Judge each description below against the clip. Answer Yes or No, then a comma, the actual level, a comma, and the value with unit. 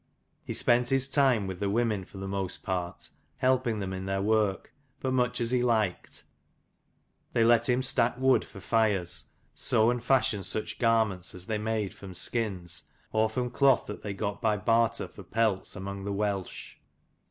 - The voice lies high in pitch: No, low, 110 Hz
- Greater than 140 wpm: Yes, average, 180 wpm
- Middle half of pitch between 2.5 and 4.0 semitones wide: Yes, average, 3.7 semitones